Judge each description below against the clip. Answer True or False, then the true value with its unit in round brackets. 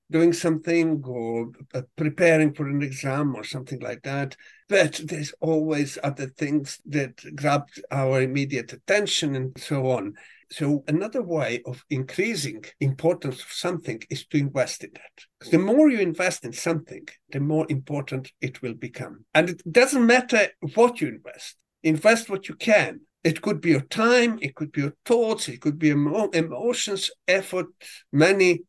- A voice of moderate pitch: True (155 Hz)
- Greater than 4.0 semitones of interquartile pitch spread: True (4.6 semitones)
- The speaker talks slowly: False (160 wpm)